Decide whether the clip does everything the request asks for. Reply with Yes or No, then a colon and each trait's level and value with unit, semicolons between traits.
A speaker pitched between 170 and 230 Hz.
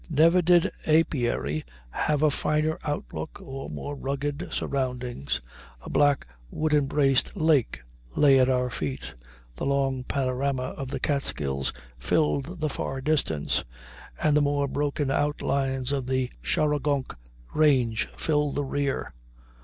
No: medium, 140 Hz